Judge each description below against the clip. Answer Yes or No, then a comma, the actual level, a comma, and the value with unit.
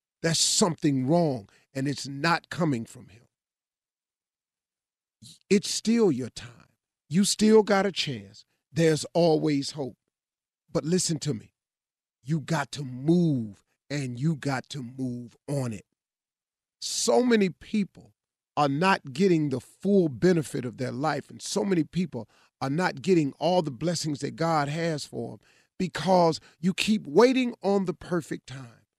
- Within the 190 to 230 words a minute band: No, average, 145 wpm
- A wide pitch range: No, average, 5.0 semitones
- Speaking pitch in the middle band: Yes, medium, 155 Hz